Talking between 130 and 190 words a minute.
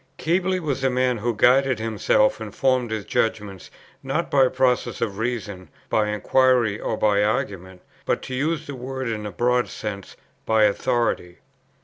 Yes: average, 160 wpm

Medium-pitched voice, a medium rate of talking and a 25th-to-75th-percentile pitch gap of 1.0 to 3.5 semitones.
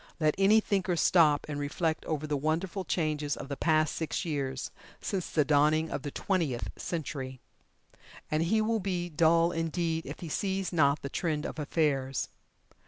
Yes: medium, 155 Hz; average, 170 wpm; average, 3.0 semitones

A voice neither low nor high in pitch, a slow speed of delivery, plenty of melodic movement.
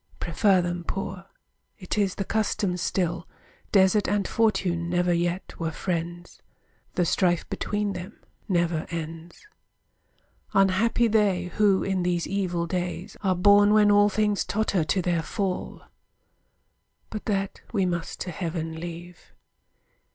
No: medium, 180 Hz; slow, 130 wpm; average, 2.7 semitones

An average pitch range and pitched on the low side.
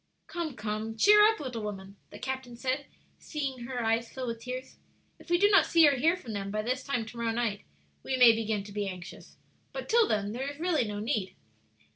No: average, 4.9 semitones; high, 245 Hz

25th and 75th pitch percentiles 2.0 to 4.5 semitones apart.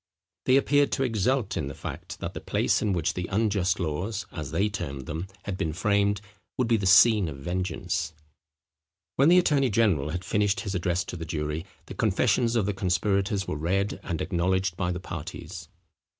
Yes: average, 3.6 semitones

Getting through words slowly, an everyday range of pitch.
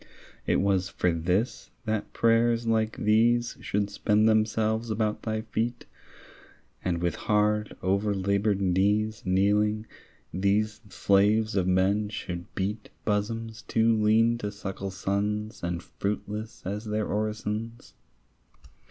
No: slow, 115 wpm; narrow, 1.8 semitones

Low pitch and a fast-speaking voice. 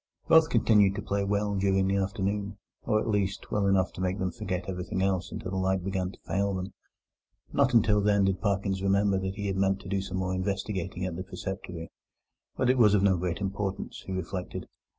Yes: very low, 95 Hz; fast, 210 wpm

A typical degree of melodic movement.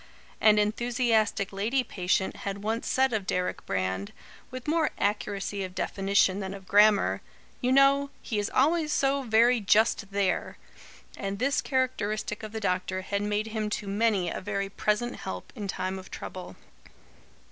Yes: average, 3.4 semitones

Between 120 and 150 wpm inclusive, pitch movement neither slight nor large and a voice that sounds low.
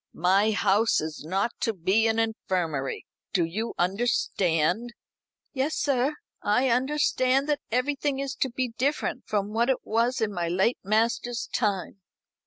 No: average, 145 wpm; average, 4.9 semitones; high, 225 Hz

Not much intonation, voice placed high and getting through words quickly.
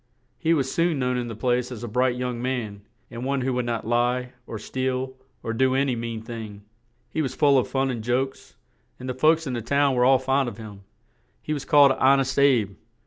No: narrow, 2.1 semitones; low, 125 Hz; fast, 230 wpm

